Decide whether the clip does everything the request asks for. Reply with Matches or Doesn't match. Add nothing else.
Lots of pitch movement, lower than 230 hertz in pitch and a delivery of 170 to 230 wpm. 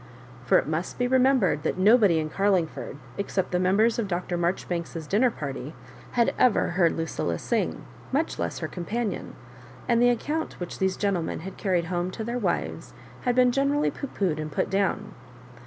Matches